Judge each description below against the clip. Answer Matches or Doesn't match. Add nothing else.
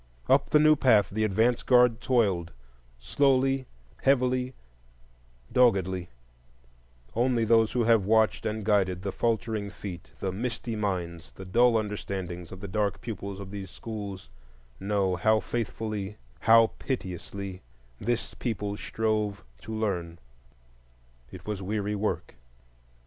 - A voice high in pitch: Doesn't match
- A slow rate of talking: Matches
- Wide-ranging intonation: Doesn't match